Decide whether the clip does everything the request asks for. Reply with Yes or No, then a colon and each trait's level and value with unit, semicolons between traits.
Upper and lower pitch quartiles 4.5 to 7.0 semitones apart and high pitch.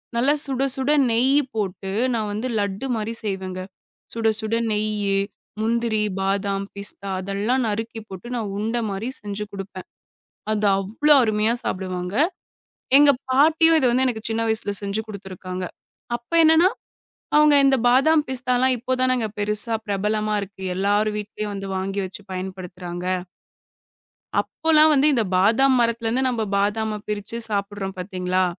No: average, 3.7 semitones; high, 215 Hz